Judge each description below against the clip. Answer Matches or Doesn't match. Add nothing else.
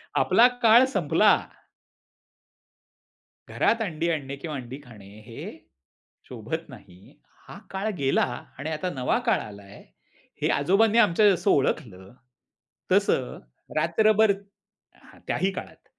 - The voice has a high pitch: Doesn't match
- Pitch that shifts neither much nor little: Doesn't match